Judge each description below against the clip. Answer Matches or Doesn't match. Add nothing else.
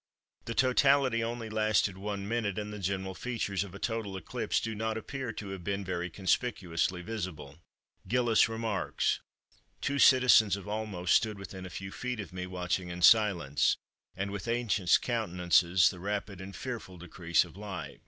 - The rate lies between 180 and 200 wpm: Doesn't match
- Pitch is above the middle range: Doesn't match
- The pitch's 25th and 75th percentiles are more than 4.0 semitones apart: Doesn't match